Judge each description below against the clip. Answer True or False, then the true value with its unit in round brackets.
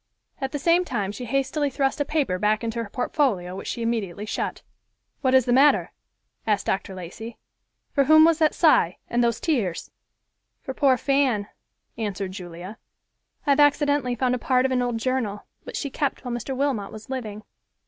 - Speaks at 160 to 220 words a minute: True (185 wpm)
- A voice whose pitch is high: True (245 Hz)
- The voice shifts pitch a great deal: False (4.8 semitones)